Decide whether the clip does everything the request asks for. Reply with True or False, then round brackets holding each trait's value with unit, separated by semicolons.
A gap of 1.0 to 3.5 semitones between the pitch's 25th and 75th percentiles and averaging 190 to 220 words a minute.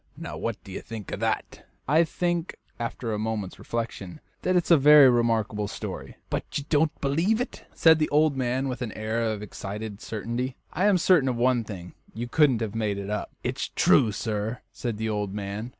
False (5.4 semitones; 200 wpm)